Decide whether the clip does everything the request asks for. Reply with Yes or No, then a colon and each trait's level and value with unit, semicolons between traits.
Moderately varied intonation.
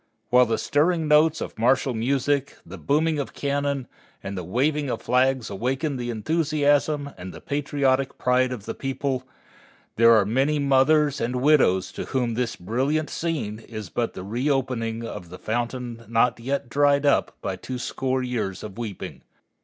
Yes: average, 3.8 semitones